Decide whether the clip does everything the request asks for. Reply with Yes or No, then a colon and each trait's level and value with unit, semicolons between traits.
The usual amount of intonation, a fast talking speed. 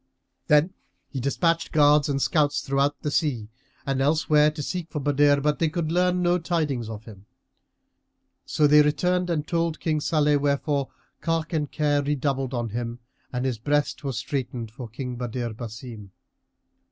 No: average, 3.4 semitones; average, 165 wpm